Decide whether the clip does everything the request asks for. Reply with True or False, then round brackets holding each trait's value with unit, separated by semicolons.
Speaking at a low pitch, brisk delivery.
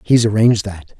False (105 Hz; 180 wpm)